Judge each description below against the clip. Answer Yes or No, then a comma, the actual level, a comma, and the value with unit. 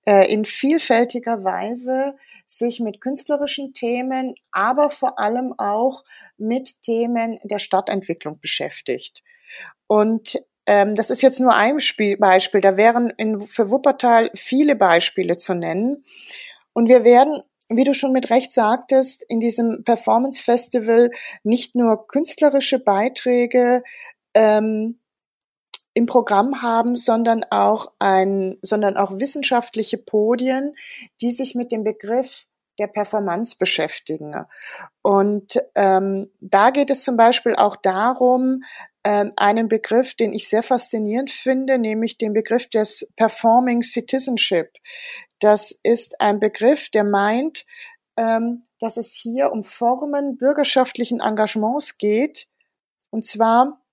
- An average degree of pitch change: Yes, average, 3.5 semitones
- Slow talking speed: Yes, slow, 120 wpm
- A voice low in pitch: No, high, 235 Hz